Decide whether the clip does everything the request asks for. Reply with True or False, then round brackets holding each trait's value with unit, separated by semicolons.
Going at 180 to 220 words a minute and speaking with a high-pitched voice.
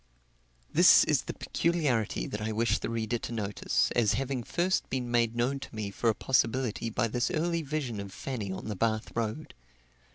False (190 wpm; 115 Hz)